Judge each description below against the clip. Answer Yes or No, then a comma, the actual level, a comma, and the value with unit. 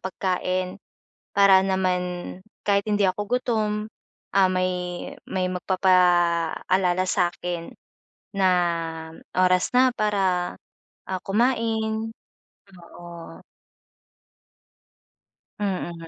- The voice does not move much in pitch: Yes, narrow, 2.0 semitones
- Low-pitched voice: No, medium, 185 Hz